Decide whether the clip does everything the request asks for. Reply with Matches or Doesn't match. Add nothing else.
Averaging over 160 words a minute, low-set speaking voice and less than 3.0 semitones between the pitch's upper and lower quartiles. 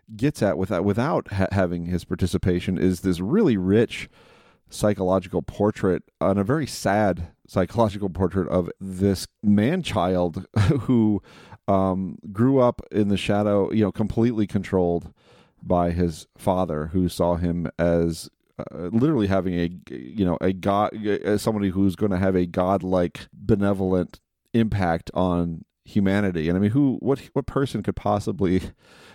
Doesn't match